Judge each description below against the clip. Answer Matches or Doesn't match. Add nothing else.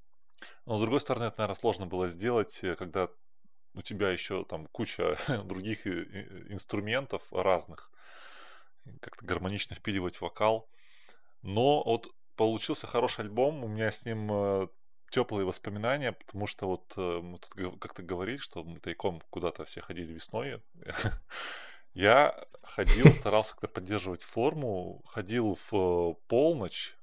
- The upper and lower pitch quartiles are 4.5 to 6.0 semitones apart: Doesn't match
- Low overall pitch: Matches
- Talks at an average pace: Matches